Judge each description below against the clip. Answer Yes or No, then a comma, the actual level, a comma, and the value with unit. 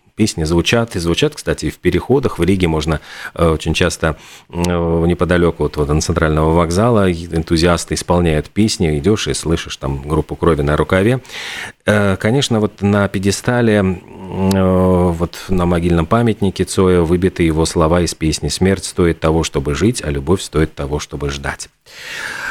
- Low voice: Yes, very low, 85 Hz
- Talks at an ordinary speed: Yes, average, 145 wpm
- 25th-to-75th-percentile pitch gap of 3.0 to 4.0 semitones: Yes, average, 3.4 semitones